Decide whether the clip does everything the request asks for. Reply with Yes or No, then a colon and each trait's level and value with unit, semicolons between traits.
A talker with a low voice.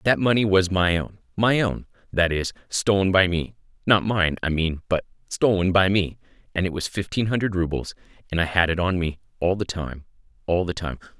Yes: very low, 90 Hz